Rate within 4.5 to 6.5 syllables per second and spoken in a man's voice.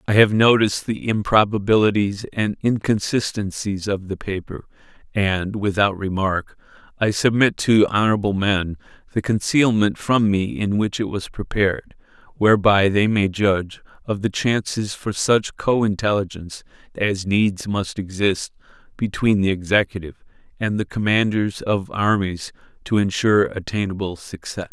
Yes: 4.7 syllables/s; male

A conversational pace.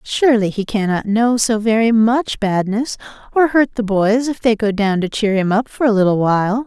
No: fast, 215 wpm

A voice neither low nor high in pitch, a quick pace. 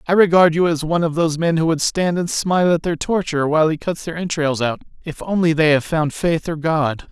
Yes: medium, 160 Hz; fast, 255 wpm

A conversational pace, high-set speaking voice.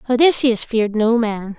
Yes: average, 150 wpm; high, 230 Hz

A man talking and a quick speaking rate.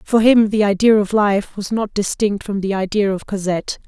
No: female; fast, 215 wpm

